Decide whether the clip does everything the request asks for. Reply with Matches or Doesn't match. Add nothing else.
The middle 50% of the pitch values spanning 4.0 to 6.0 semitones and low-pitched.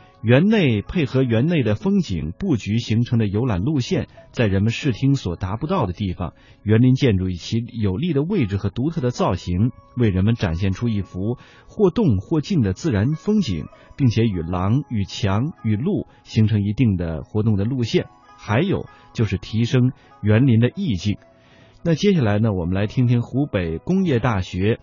Matches